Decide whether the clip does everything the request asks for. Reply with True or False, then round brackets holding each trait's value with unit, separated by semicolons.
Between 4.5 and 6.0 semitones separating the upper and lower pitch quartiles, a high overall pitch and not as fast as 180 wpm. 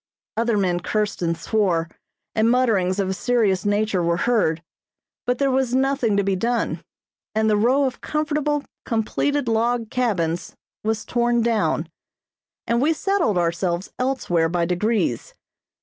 True (5.1 semitones; 220 Hz; 145 wpm)